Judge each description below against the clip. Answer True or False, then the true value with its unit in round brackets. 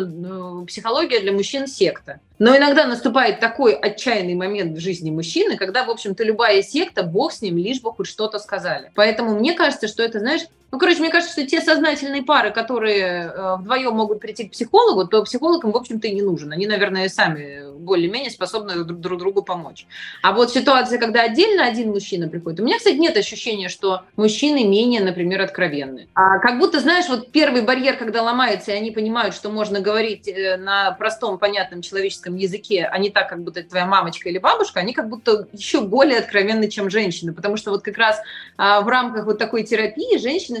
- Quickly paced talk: True (190 wpm)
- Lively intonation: False (4.3 semitones)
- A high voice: True (215 Hz)